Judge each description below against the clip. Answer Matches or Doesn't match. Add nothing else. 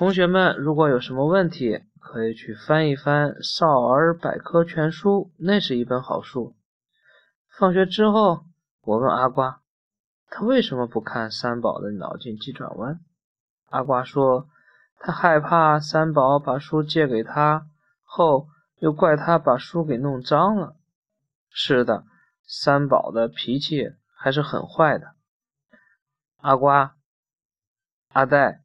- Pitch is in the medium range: Matches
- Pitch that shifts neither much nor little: Matches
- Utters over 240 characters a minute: Doesn't match